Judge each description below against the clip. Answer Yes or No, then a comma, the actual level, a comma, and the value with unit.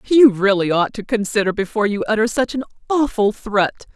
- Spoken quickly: No, average, 180 wpm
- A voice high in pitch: Yes, high, 215 Hz